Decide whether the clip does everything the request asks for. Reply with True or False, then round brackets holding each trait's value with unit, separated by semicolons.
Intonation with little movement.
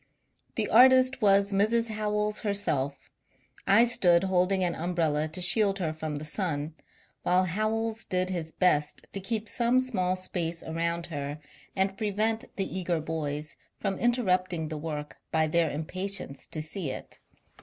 False (4.7 semitones)